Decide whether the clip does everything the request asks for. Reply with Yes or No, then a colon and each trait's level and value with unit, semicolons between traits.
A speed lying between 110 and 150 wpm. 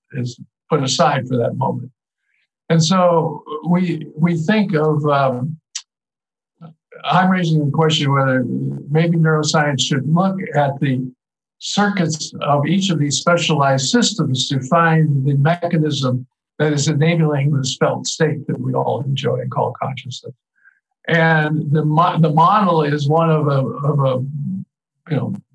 Yes: average, 145 wpm